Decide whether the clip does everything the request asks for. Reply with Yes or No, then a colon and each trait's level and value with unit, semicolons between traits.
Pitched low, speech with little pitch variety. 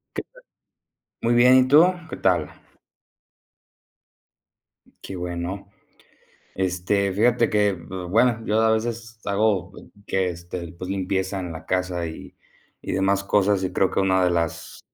No: very low, 95 Hz; average, 3.4 semitones